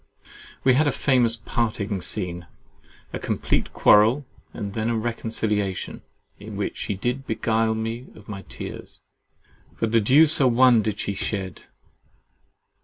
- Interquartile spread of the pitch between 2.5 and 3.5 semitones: Yes, average, 2.9 semitones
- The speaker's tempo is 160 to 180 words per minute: No, average, 140 wpm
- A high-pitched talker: No, low, 110 Hz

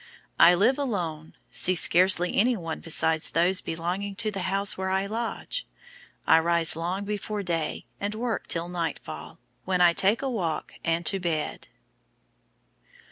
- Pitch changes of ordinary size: Yes, average, 3.3 semitones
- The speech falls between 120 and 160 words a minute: Yes, average, 145 wpm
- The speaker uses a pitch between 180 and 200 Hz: Yes, medium, 185 Hz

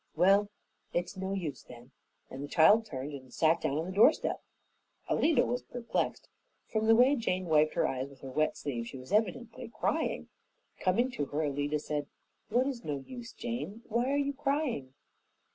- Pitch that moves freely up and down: Yes, wide, 8.6 semitones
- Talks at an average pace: Yes, average, 180 wpm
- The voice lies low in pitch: No, medium, 185 Hz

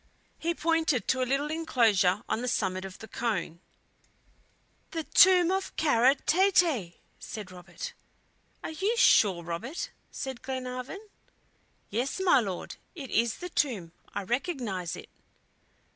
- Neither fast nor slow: No, slow, 130 wpm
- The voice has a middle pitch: No, very high, 255 Hz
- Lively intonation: Yes, wide, 8.5 semitones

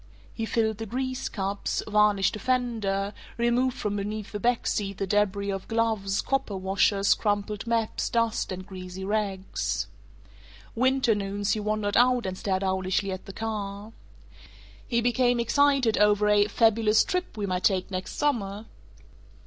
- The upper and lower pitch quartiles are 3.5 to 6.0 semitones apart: No, average, 2.7 semitones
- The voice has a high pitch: Yes, high, 210 Hz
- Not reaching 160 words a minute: Yes, average, 150 wpm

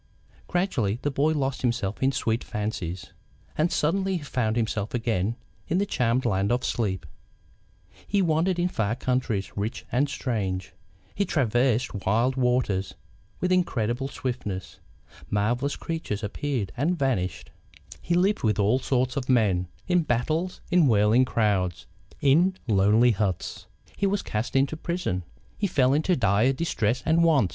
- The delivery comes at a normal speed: Yes, average, 145 wpm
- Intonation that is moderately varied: No, wide, 6.6 semitones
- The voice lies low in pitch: Yes, low, 125 Hz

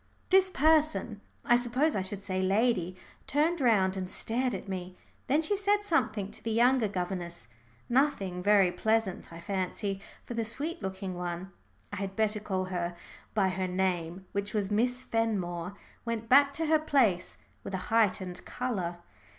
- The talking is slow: No, average, 165 wpm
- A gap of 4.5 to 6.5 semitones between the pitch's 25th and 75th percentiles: Yes, average, 4.9 semitones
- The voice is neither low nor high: No, high, 205 Hz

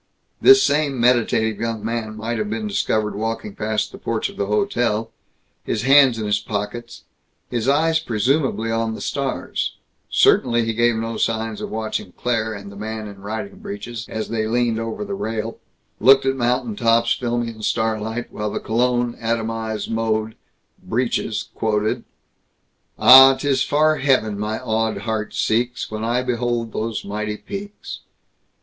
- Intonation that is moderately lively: No, narrow, 2.2 semitones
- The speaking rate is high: No, average, 160 wpm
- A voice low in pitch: Yes, low, 115 Hz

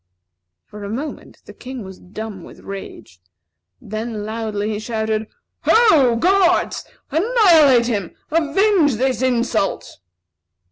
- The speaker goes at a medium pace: No, slow, 110 wpm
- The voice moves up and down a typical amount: No, wide, 6.3 semitones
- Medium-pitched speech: No, high, 235 Hz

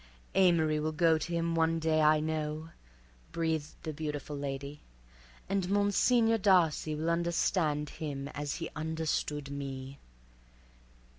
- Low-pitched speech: No, medium, 155 Hz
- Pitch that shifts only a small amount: Yes, narrow, 2.1 semitones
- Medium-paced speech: No, slow, 125 wpm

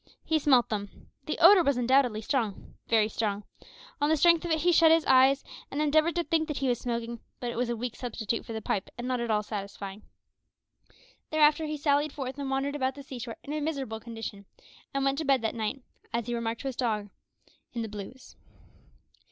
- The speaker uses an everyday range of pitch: Yes, average, 4.4 semitones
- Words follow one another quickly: Yes, fast, 215 wpm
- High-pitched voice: Yes, very high, 255 Hz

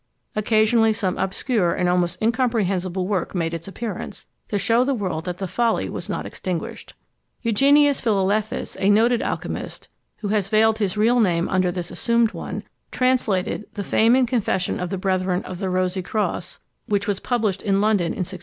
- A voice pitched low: No, high, 200 Hz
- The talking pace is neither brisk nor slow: Yes, average, 175 wpm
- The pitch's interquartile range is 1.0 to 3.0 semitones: No, average, 3.4 semitones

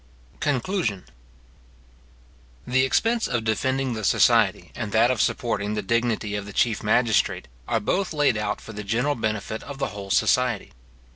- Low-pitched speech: Yes, low, 115 Hz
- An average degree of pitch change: Yes, average, 3.6 semitones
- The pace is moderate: Yes, average, 155 wpm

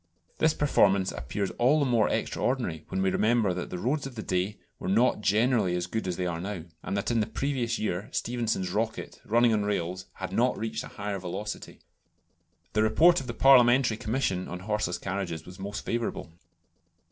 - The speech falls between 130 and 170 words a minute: No, average, 185 wpm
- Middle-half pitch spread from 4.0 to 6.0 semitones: Yes, average, 4.3 semitones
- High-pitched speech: No, low, 105 Hz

